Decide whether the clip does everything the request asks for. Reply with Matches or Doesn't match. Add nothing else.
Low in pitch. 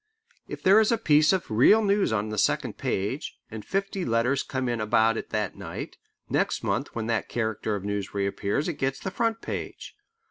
Matches